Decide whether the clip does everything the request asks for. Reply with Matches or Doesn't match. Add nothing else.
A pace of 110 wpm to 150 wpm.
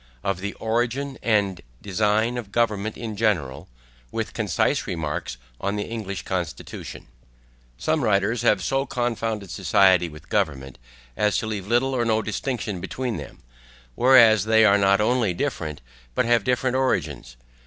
Matches